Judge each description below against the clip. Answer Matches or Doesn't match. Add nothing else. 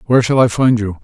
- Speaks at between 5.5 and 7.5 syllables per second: Matches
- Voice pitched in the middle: Doesn't match